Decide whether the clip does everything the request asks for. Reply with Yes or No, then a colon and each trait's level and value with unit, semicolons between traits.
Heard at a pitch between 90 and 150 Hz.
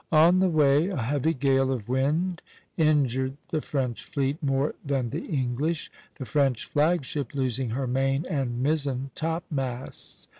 Yes: medium, 140 Hz